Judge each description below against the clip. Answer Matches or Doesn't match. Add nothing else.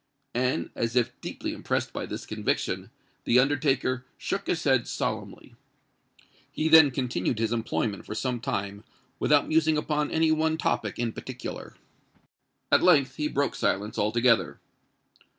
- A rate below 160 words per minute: Matches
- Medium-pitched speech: Doesn't match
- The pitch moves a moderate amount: Matches